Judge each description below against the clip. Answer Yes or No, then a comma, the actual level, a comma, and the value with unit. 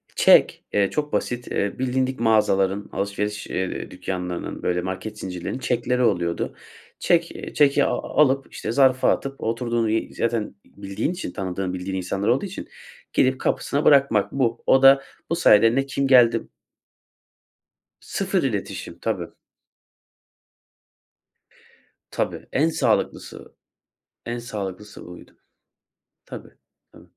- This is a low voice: Yes, low, 115 Hz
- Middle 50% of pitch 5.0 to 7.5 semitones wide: Yes, average, 5.3 semitones